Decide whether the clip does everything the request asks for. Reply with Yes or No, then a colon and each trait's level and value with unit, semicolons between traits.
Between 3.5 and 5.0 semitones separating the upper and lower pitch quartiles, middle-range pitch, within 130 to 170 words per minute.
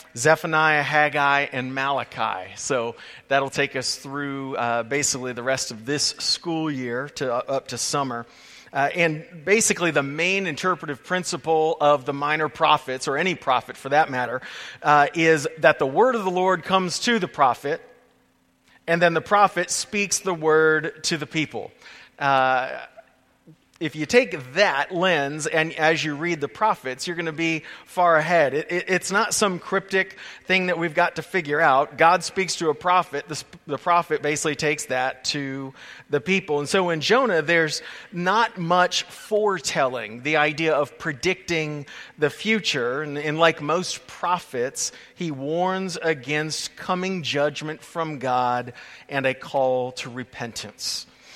Yes: average, 3.8 semitones; medium, 155 Hz; average, 160 wpm